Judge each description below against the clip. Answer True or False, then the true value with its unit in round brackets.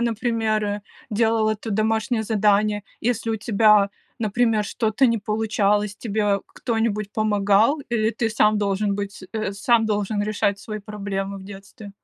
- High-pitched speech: True (215 Hz)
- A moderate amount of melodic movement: False (1.6 semitones)